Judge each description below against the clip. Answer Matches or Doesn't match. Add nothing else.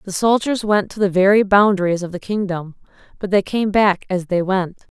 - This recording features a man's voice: Doesn't match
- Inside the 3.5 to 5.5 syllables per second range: Matches